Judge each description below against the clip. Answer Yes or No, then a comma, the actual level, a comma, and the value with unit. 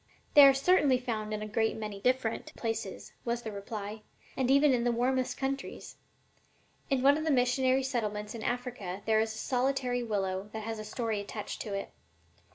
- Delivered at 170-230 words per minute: Yes, average, 185 wpm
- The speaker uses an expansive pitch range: No, average, 3.4 semitones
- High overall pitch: Yes, high, 235 Hz